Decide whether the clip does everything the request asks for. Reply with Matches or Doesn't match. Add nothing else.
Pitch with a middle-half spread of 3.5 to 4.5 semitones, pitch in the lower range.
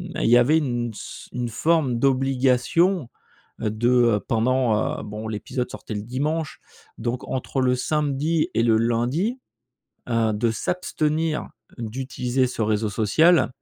Matches